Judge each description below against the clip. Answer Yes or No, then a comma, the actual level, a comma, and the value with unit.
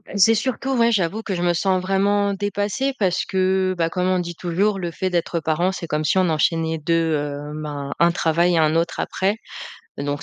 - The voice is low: No, medium, 180 Hz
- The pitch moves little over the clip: No, average, 3.1 semitones